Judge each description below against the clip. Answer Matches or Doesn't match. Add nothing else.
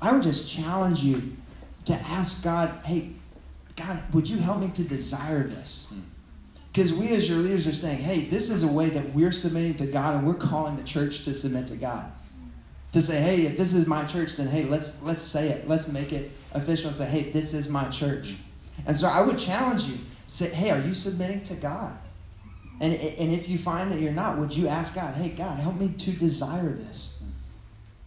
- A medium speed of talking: Doesn't match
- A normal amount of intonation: Matches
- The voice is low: Doesn't match